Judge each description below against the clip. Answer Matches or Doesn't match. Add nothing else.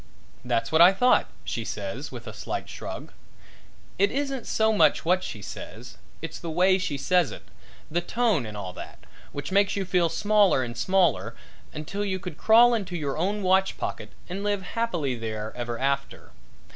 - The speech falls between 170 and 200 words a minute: Matches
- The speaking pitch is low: Doesn't match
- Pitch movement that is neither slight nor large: Doesn't match